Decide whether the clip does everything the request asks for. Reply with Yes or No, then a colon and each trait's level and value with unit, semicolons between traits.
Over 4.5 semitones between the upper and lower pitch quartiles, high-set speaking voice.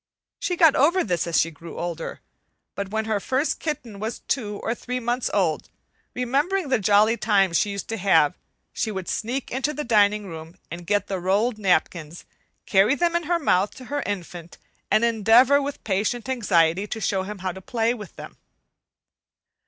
Yes: average, 5.0 semitones; high, 210 Hz